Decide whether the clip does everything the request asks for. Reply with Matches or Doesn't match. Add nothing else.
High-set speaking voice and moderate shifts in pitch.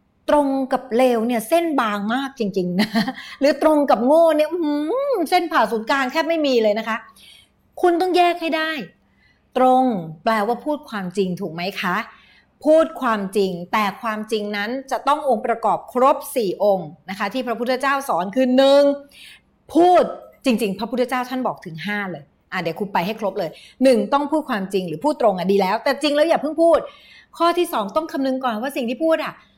Doesn't match